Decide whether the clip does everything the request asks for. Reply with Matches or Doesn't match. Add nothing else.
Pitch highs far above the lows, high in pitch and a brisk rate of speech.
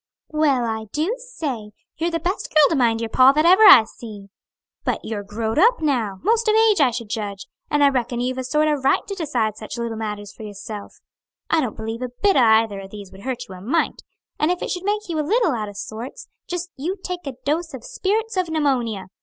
Matches